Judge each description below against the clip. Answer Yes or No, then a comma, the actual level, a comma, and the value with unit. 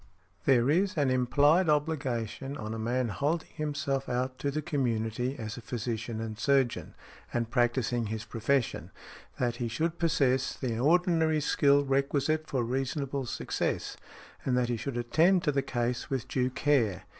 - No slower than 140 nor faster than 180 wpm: Yes, average, 155 wpm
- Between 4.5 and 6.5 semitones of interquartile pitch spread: No, average, 3.4 semitones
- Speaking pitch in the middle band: No, low, 130 Hz